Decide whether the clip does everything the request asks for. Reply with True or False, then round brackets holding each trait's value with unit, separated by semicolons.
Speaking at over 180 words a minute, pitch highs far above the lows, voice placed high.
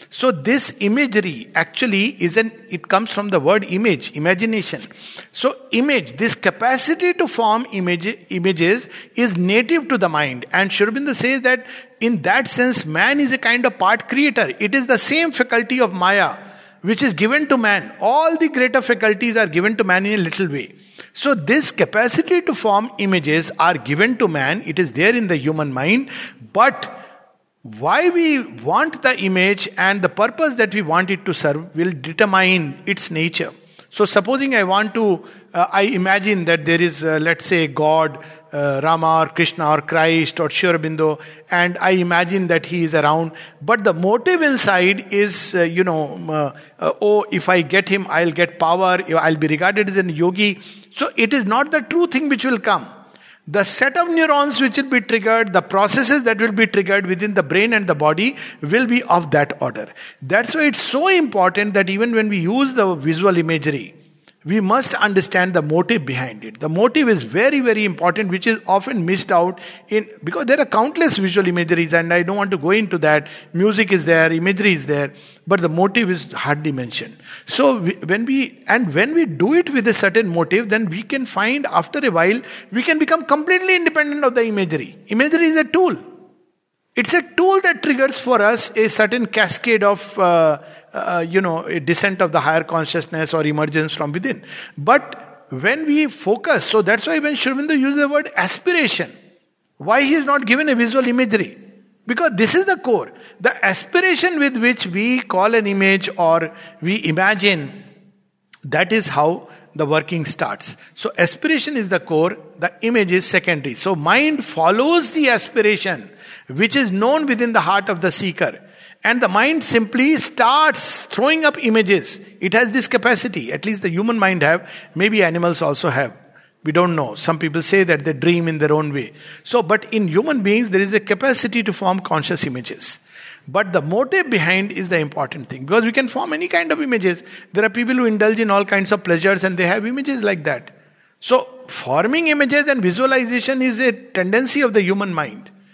True (190 wpm; 6.3 semitones; 205 Hz)